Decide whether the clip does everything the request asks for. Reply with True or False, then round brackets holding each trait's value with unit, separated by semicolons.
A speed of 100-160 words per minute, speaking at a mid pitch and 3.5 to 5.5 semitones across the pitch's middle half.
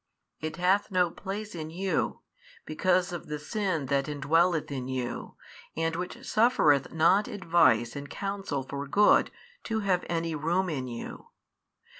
True (145 wpm; 165 Hz; 4.9 semitones)